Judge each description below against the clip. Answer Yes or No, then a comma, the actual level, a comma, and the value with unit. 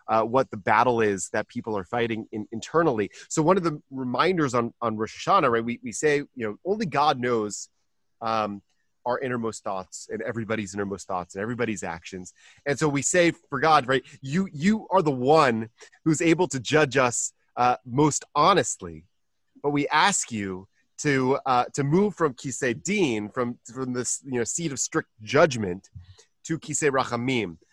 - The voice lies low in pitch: Yes, low, 125 Hz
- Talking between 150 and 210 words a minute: Yes, average, 180 wpm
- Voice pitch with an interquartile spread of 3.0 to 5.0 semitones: No, wide, 5.4 semitones